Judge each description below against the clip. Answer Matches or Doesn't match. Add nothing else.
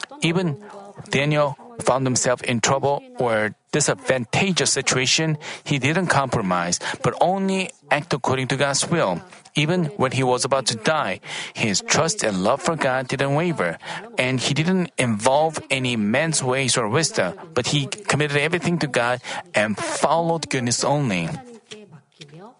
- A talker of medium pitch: Matches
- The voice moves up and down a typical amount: Matches